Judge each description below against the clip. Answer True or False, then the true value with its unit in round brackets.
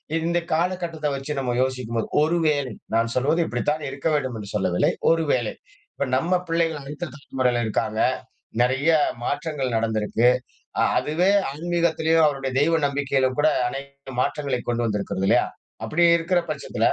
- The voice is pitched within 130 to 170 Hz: True (140 Hz)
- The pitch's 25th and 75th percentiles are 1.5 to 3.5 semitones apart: False (4.5 semitones)